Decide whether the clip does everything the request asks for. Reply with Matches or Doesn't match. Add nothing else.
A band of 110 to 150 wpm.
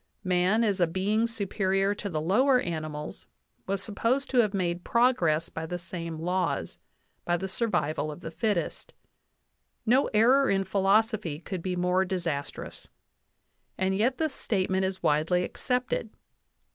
Matches